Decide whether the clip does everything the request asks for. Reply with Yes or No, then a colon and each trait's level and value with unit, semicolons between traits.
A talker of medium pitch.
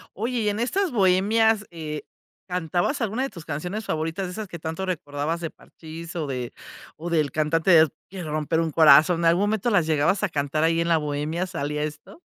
Yes: medium, 165 Hz